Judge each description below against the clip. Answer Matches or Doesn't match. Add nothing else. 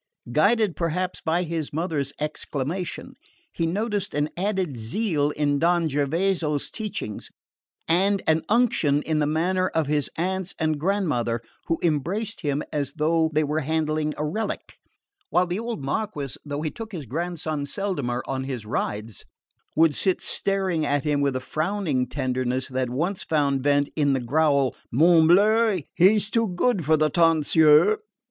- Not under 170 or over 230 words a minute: Doesn't match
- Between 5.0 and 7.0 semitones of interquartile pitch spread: Doesn't match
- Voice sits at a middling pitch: Matches